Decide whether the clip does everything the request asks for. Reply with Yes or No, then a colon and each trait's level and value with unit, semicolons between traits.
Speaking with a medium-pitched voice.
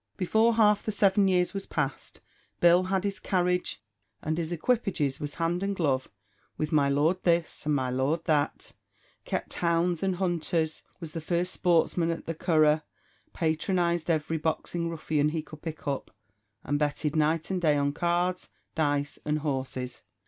Yes: medium, 165 Hz